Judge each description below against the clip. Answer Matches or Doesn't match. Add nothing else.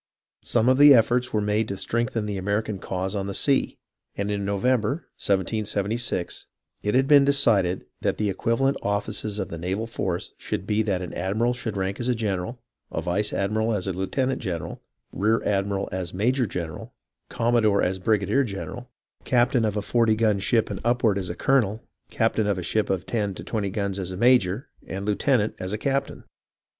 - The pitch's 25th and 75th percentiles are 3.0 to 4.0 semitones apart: Matches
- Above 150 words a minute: Matches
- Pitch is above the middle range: Doesn't match